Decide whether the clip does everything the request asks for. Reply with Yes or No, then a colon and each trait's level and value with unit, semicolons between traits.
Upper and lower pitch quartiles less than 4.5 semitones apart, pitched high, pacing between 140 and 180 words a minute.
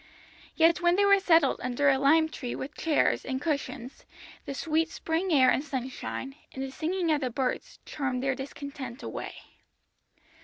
Yes: average, 3.6 semitones; very high, 280 Hz; average, 165 wpm